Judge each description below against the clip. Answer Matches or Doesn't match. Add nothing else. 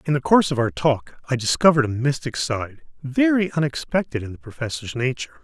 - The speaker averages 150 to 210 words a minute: Matches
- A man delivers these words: Matches